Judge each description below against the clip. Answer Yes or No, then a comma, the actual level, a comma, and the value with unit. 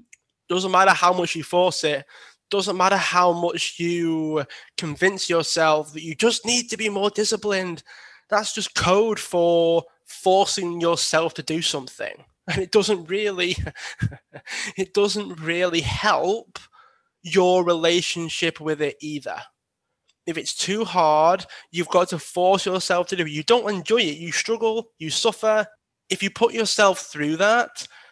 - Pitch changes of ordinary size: Yes, average, 3.6 semitones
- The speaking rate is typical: Yes, average, 150 wpm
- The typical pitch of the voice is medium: Yes, medium, 180 Hz